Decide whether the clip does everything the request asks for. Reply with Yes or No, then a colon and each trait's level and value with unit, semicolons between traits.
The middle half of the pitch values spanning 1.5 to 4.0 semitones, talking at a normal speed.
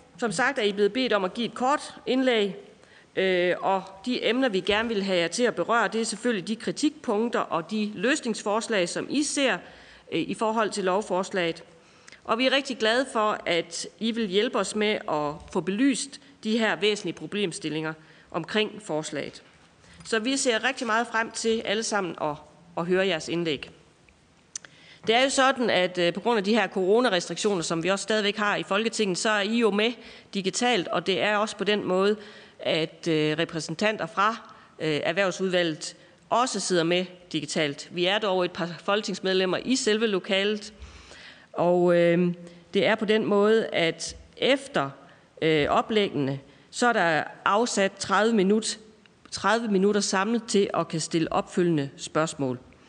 No: average, 4.4 semitones; average, 165 wpm